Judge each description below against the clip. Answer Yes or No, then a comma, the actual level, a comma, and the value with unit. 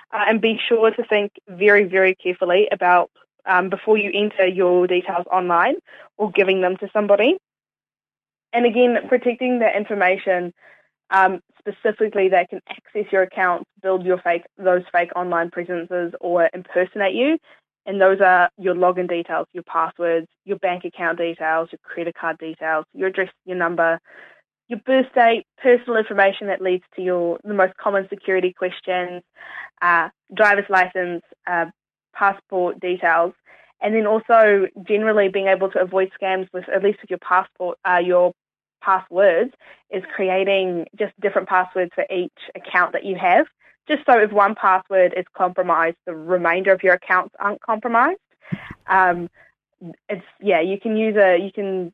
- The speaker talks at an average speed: Yes, average, 160 wpm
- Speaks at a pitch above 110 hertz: Yes, high, 190 Hz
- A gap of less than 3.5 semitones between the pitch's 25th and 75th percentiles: Yes, narrow, 2.5 semitones